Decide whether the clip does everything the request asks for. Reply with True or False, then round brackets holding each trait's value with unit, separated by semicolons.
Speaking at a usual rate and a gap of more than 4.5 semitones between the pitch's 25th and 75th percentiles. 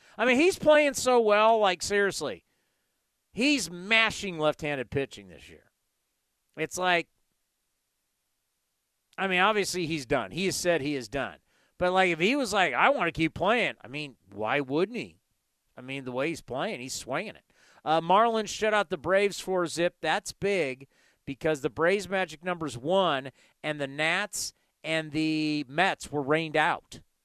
True (175 wpm; 5.1 semitones)